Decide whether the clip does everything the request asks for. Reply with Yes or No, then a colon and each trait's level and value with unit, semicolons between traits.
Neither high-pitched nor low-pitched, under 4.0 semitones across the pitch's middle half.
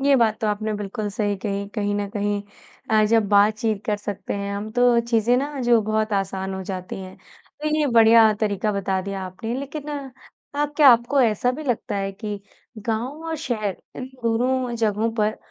No: high, 215 Hz; average, 3.0 semitones